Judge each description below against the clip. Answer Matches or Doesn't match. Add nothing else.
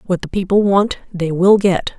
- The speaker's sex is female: Matches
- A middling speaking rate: Doesn't match